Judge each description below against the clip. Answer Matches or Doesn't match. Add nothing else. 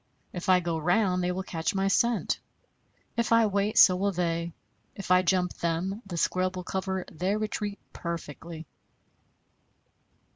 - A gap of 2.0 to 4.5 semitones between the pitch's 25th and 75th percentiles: Matches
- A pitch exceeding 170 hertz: Matches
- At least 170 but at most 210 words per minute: Doesn't match